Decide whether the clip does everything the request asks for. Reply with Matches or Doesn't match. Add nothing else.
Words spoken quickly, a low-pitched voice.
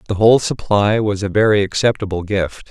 Doesn't match